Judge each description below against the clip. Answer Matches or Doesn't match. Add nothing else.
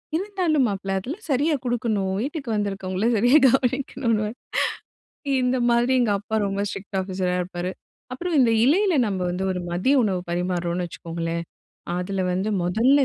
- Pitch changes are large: Matches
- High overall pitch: Matches